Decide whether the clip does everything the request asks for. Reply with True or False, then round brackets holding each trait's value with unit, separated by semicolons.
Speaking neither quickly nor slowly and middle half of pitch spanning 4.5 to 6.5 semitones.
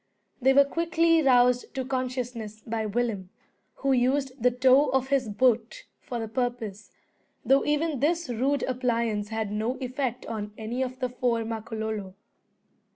False (150 wpm; 3.1 semitones)